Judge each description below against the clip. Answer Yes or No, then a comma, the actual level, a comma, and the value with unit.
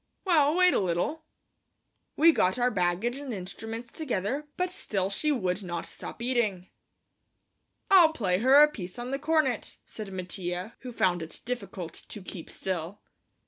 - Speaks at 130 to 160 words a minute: Yes, average, 155 wpm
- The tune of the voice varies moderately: No, wide, 7.4 semitones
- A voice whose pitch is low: No, high, 225 Hz